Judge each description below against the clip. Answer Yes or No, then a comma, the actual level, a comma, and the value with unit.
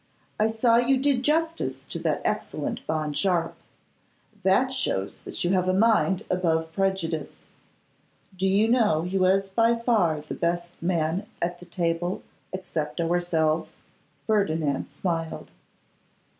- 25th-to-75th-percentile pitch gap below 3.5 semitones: No, average, 4.7 semitones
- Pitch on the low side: No, medium, 185 Hz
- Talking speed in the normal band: No, slow, 130 wpm